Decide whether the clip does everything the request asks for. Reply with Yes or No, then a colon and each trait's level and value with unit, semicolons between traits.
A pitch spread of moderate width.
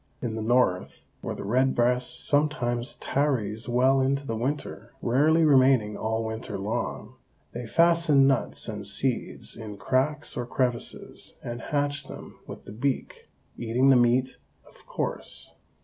Yes: average, 3.3 semitones